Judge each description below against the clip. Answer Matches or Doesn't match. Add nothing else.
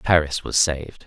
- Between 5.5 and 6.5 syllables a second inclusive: Doesn't match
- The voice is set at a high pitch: Doesn't match